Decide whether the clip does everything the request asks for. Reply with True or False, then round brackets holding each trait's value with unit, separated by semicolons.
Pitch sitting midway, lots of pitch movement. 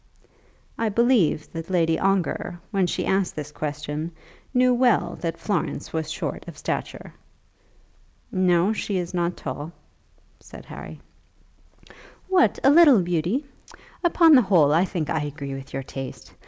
True (175 Hz; 5.7 semitones)